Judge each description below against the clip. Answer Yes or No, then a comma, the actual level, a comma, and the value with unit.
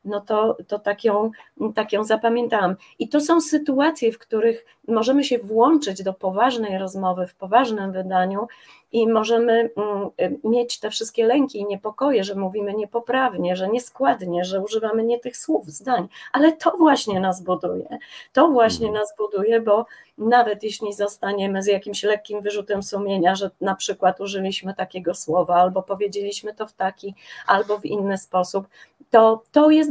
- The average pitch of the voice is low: No, high, 210 Hz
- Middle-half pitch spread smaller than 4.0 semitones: Yes, average, 3.0 semitones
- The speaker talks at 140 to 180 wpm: Yes, average, 155 wpm